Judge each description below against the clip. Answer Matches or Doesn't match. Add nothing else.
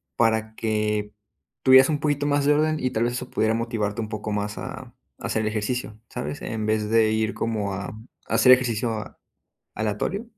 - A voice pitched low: Matches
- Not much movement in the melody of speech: Doesn't match